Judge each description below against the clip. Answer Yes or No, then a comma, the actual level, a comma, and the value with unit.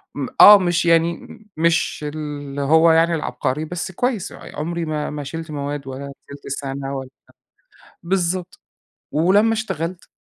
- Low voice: No, medium, 160 Hz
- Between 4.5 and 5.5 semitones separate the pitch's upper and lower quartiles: No, average, 3.3 semitones